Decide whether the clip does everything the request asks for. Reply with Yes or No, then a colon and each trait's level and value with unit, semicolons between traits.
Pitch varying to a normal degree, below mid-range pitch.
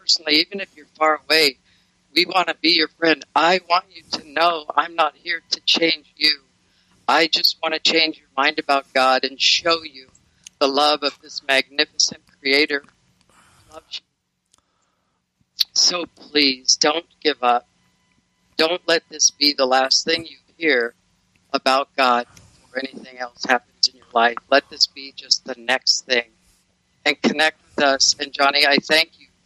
No: average, 3.1 semitones; medium, 145 Hz